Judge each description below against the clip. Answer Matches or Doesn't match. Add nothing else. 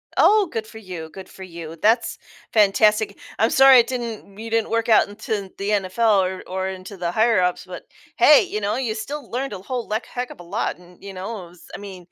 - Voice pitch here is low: Doesn't match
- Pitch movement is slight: Doesn't match